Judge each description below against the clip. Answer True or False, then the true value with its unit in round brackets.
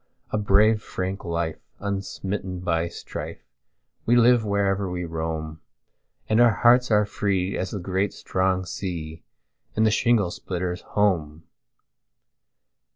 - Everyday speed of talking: False (110 wpm)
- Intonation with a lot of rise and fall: False (3.3 semitones)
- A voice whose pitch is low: True (95 Hz)